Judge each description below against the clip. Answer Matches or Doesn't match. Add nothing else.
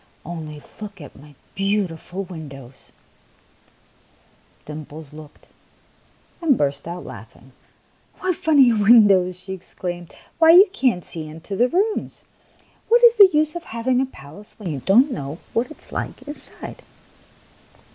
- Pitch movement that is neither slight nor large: Doesn't match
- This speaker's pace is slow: Doesn't match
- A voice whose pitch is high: Matches